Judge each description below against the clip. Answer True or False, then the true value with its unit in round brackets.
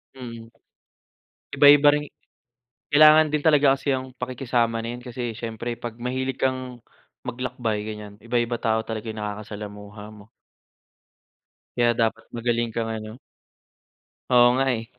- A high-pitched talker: False (120 Hz)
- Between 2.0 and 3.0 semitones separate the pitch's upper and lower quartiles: True (2.6 semitones)